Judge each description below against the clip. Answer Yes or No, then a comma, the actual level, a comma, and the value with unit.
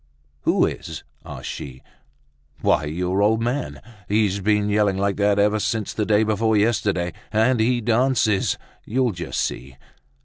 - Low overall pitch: Yes, low, 105 Hz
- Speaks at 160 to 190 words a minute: No, average, 145 wpm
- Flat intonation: Yes, narrow, 2.1 semitones